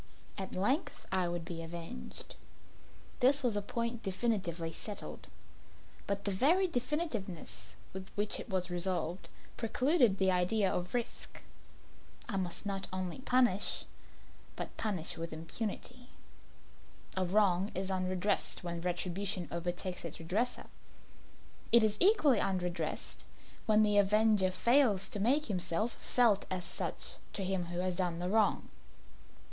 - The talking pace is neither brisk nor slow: No, slow, 130 wpm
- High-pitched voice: Yes, high, 195 Hz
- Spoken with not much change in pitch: No, average, 4.1 semitones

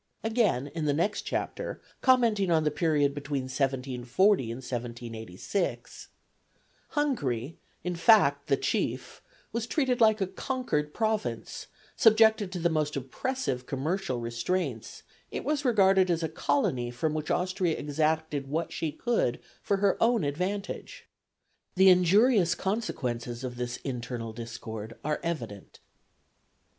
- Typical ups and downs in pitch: No, wide, 7.9 semitones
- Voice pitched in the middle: Yes, medium, 155 Hz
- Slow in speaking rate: Yes, slow, 130 wpm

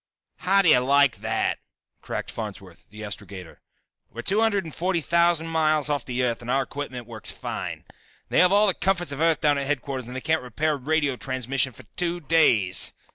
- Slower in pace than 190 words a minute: No, average, 195 wpm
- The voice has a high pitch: No, medium, 140 Hz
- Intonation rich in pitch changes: No, average, 4.9 semitones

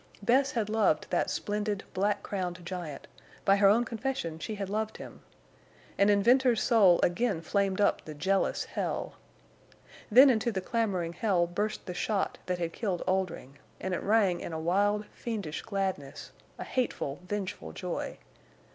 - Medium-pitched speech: No, high, 200 Hz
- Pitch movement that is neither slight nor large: Yes, average, 3.6 semitones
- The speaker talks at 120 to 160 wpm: Yes, average, 155 wpm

